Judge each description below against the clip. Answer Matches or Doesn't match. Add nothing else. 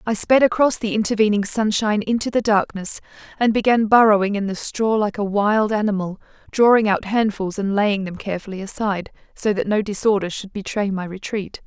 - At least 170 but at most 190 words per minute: Matches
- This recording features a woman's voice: Matches